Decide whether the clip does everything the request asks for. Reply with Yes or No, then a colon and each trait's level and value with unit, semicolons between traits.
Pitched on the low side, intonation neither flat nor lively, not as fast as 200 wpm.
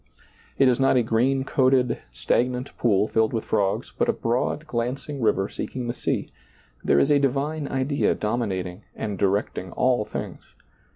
Yes: low, 120 Hz; average, 3.9 semitones; average, 165 wpm